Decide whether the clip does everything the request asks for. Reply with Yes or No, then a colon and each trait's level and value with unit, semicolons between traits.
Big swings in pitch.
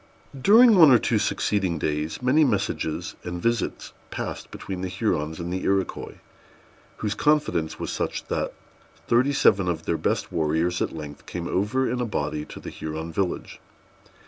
Yes: wide, 6.7 semitones